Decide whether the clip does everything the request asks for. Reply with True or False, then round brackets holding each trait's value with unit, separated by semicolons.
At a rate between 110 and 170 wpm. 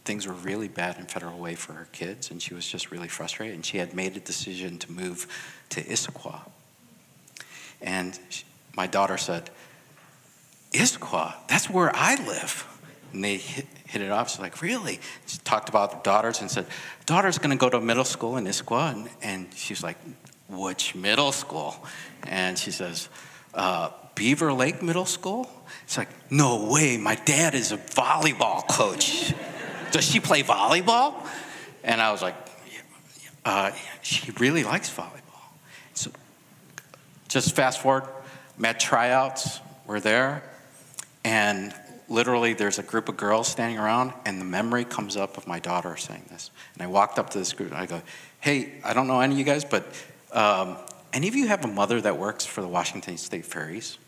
False (180 wpm)